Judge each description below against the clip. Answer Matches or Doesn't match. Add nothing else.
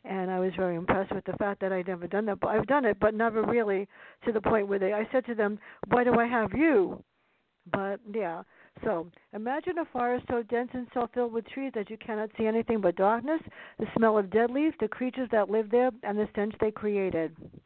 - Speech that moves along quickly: Matches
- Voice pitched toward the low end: Doesn't match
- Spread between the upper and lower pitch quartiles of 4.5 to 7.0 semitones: Doesn't match